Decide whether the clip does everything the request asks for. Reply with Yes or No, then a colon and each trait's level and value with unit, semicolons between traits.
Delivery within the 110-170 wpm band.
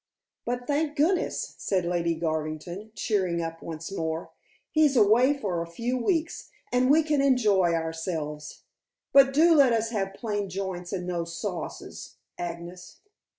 Yes: average, 145 wpm